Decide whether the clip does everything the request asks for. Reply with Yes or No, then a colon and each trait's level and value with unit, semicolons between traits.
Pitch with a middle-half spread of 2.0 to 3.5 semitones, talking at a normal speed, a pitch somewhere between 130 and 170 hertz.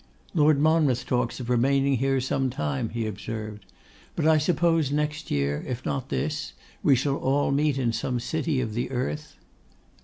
No: average, 4.0 semitones; average, 165 wpm; low, 135 Hz